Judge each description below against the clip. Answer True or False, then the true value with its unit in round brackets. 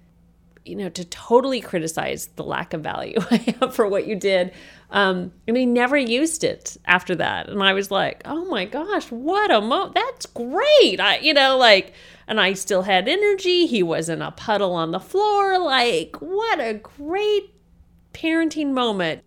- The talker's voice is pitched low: False (240 Hz)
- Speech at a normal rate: True (180 wpm)